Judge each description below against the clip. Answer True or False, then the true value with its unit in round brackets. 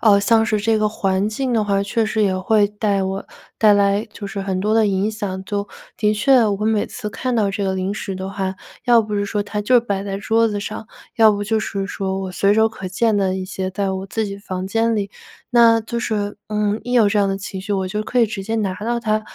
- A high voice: True (205 Hz)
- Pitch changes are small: True (2.1 semitones)